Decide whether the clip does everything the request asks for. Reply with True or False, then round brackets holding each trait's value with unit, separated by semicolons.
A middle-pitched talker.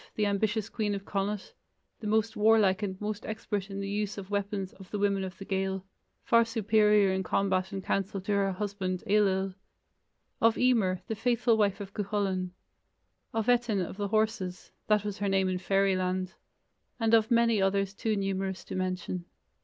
False (200 Hz)